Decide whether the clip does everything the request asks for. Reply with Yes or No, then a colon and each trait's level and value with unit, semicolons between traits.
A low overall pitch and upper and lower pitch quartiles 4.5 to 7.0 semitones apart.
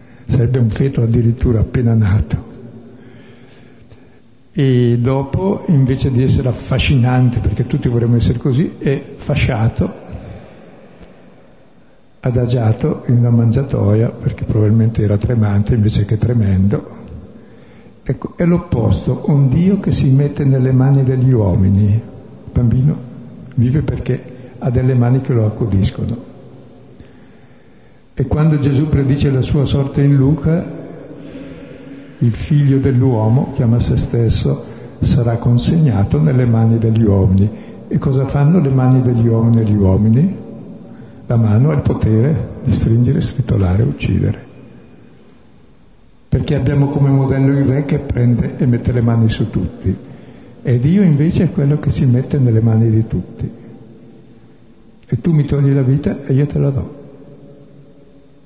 No: low, 125 Hz; average, 3.3 semitones